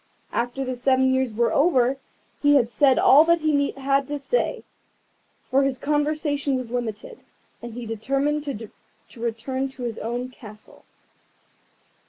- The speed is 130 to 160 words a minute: Yes, average, 145 wpm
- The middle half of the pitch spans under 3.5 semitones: Yes, average, 3.0 semitones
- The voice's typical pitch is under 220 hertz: No, very high, 260 Hz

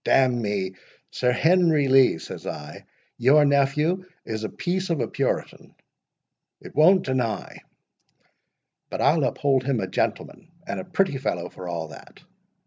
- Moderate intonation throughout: No, wide, 6.2 semitones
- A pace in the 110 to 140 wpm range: Yes, slow, 135 wpm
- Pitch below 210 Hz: Yes, low, 135 Hz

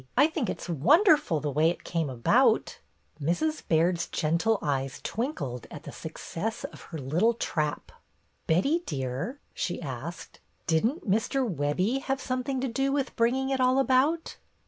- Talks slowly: No, average, 155 wpm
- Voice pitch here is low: No, high, 200 Hz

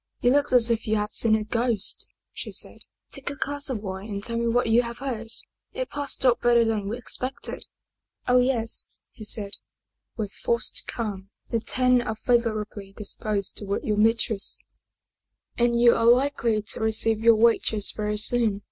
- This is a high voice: Yes, high, 230 Hz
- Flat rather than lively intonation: Yes, narrow, 2.3 semitones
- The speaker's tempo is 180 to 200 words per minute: Yes, average, 190 wpm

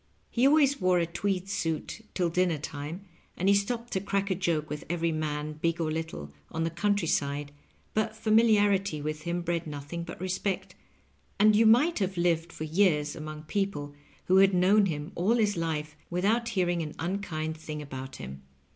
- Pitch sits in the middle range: Yes, medium, 175 Hz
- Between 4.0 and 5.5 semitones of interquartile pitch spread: Yes, average, 4.4 semitones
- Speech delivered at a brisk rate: No, average, 180 wpm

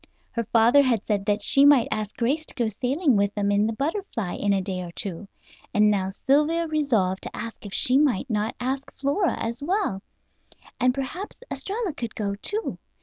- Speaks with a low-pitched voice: No, high, 235 Hz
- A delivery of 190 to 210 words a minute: Yes, average, 195 wpm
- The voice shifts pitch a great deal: Yes, wide, 5.8 semitones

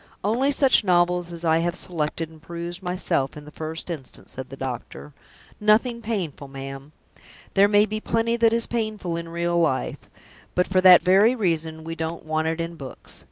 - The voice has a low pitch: No, medium, 170 Hz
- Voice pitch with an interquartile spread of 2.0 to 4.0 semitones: No, average, 4.5 semitones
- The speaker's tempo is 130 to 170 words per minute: No, average, 185 wpm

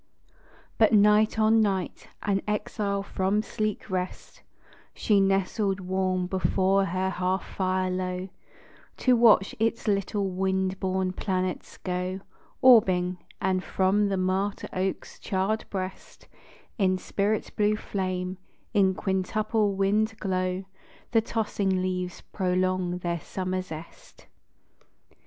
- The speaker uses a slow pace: Yes, slow, 115 wpm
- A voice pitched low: No, high, 190 Hz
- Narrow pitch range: Yes, narrow, 1.9 semitones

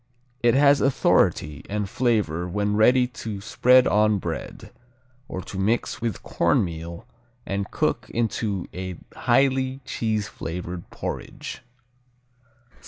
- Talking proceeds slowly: Yes, slow, 110 wpm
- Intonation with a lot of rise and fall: No, average, 4.8 semitones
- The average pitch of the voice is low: Yes, low, 105 Hz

